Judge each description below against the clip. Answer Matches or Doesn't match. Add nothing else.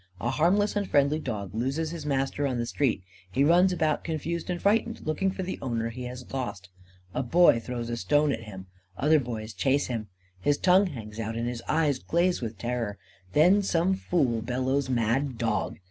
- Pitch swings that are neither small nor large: Doesn't match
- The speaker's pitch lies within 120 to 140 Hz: Matches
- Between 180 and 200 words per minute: Matches